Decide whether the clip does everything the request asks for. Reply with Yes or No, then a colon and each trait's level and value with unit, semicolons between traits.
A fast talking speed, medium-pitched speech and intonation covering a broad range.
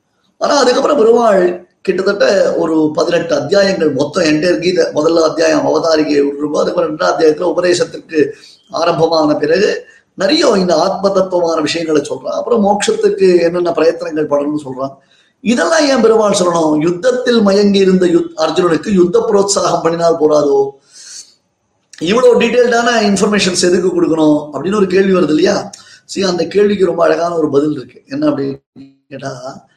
No: fast, 135 wpm; medium, 175 Hz; average, 4.4 semitones